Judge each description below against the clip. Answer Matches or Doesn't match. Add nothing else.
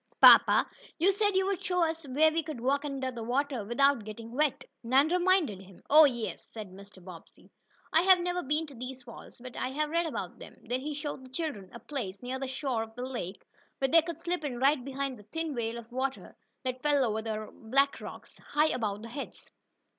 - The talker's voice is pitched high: Matches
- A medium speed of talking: Doesn't match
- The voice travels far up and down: Doesn't match